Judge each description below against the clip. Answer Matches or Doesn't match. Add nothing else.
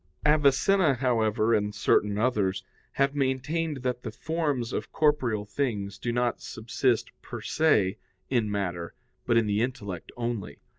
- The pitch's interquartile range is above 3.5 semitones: Matches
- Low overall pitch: Matches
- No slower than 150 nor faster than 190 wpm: Doesn't match